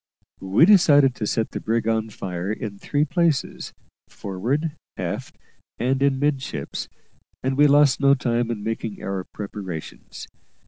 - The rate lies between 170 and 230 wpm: No, average, 140 wpm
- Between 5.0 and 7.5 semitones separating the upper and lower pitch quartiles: Yes, wide, 5.4 semitones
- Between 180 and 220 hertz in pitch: No, low, 120 Hz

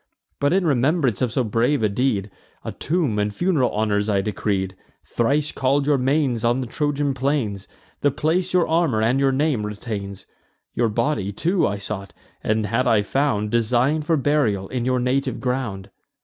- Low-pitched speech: Yes, low, 125 Hz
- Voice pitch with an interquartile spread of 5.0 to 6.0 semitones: Yes, wide, 5.4 semitones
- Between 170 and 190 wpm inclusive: Yes, average, 175 wpm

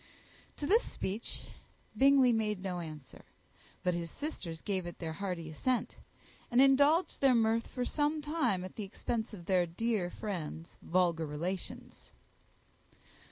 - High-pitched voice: Yes, high, 200 Hz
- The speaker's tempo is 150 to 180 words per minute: No, average, 140 wpm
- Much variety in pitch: Yes, wide, 6.7 semitones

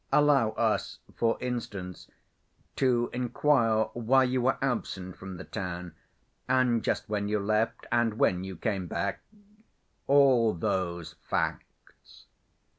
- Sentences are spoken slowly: Yes, slow, 115 wpm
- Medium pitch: No, low, 115 Hz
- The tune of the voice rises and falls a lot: No, average, 4.9 semitones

